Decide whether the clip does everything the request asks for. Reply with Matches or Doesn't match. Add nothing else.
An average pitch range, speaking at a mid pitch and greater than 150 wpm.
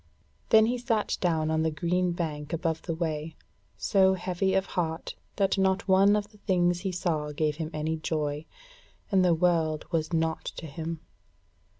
Matches